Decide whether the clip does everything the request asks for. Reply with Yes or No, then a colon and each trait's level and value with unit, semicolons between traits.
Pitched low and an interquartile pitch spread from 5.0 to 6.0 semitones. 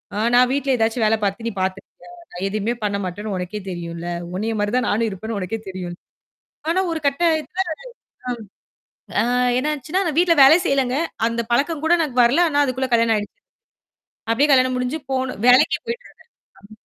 No: high, 245 Hz; wide, 5.5 semitones